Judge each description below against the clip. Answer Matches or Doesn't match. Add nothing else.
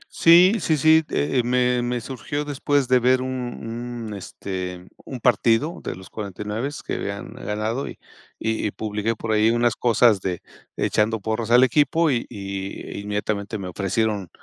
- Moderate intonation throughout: Matches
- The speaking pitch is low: Matches